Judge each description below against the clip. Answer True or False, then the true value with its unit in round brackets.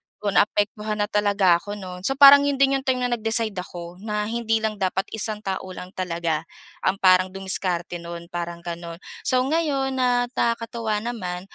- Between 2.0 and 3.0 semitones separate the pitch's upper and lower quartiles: False (4.3 semitones)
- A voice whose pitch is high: True (205 Hz)